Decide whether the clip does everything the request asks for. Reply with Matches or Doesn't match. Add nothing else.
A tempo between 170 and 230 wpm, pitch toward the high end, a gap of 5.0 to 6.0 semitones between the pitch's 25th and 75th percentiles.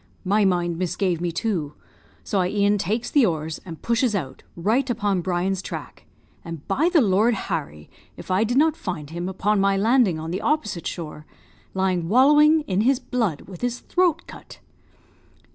Matches